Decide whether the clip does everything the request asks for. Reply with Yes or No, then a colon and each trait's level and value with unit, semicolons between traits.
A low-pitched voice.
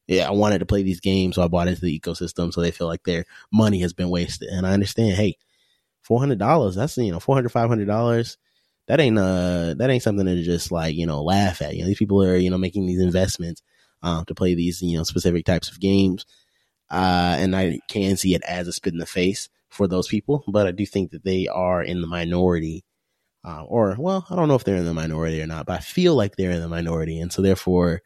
Yes: very low, 90 Hz